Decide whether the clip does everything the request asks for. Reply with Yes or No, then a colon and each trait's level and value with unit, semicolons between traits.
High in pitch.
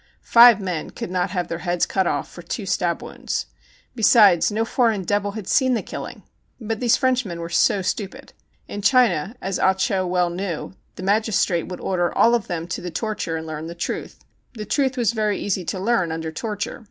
Yes: high, 195 Hz